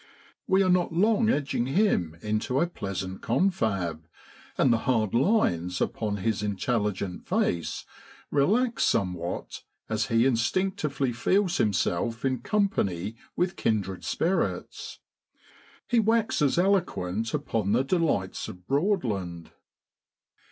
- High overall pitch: No, low, 115 Hz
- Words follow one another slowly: Yes, slow, 110 wpm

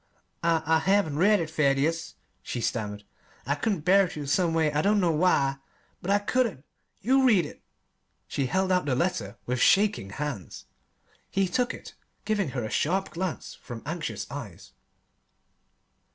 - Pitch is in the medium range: Yes, medium, 165 Hz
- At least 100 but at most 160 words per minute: Yes, average, 155 wpm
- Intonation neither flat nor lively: No, wide, 5.9 semitones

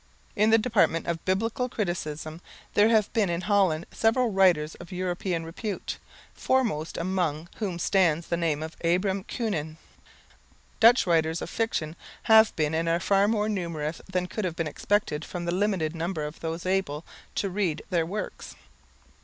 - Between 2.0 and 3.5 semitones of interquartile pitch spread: No, average, 4.0 semitones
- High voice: No, medium, 180 Hz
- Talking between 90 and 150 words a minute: No, average, 160 wpm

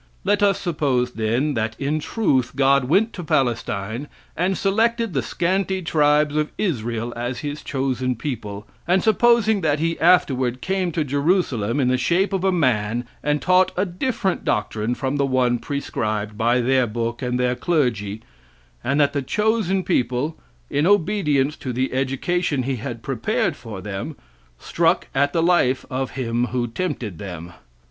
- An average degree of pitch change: No, wide, 6.4 semitones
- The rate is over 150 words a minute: Yes, average, 160 wpm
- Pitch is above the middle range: No, low, 135 Hz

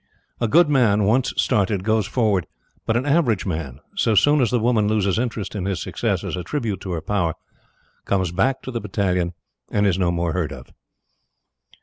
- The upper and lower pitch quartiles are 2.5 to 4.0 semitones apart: No, average, 4.4 semitones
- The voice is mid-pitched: No, low, 105 Hz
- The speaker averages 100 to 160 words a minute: No, average, 195 wpm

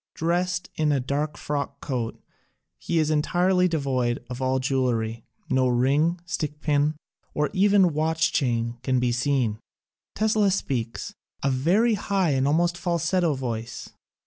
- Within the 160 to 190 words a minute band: No, slow, 135 wpm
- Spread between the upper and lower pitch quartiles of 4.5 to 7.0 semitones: Yes, average, 5.2 semitones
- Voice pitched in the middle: Yes, medium, 145 Hz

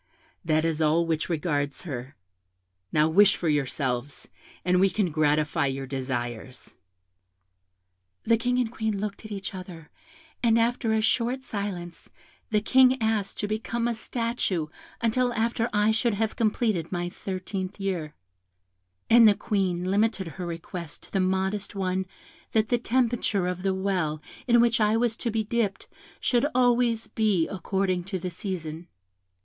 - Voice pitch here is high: Yes, high, 195 Hz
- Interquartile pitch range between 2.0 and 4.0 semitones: No, average, 5.0 semitones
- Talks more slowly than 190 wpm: Yes, average, 155 wpm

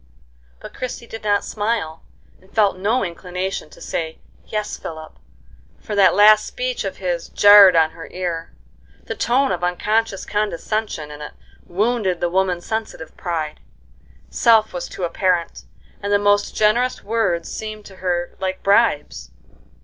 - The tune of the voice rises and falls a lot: No, average, 3.7 semitones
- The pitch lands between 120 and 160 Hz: No, high, 195 Hz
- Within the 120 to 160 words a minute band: Yes, average, 150 wpm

